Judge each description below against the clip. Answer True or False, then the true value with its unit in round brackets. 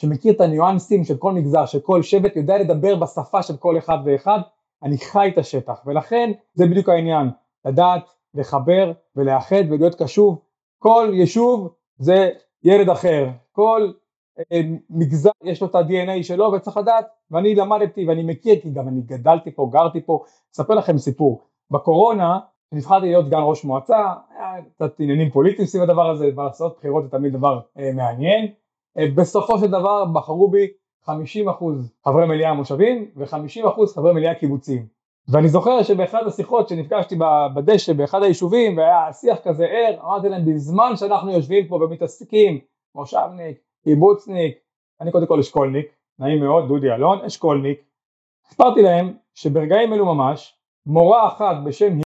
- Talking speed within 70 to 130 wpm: False (145 wpm)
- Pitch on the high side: False (170 Hz)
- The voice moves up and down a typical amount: True (4.9 semitones)